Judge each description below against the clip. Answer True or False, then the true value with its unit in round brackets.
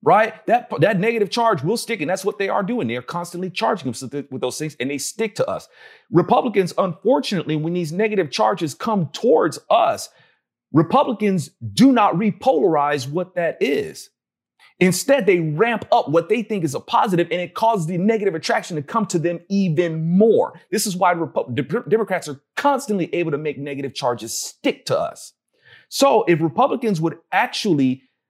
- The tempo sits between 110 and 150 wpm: False (180 wpm)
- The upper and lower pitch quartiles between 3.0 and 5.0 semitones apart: False (5.6 semitones)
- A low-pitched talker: False (180 Hz)